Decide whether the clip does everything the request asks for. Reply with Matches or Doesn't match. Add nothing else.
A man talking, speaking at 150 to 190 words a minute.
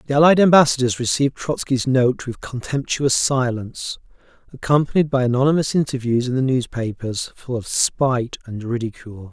Doesn't match